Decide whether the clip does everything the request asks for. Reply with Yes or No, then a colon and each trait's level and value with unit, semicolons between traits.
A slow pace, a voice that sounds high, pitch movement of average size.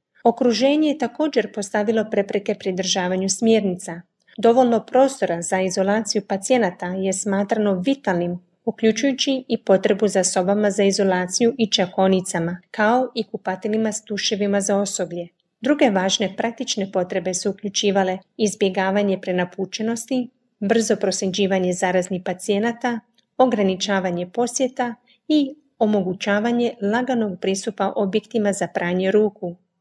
Yes: slow, 105 wpm; high, 205 Hz; average, 3.5 semitones